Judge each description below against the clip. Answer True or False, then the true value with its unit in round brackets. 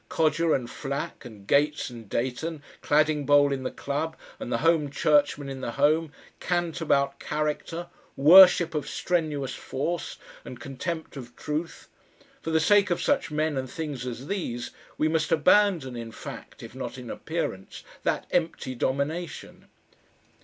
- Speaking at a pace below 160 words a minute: True (150 wpm)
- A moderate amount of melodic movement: True (3.6 semitones)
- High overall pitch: False (150 Hz)